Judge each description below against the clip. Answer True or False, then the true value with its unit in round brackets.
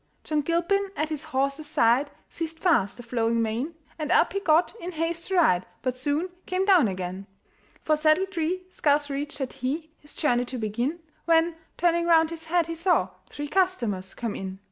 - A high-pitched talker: True (310 Hz)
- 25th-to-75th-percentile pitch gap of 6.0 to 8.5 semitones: False (5.4 semitones)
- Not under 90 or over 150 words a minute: False (185 wpm)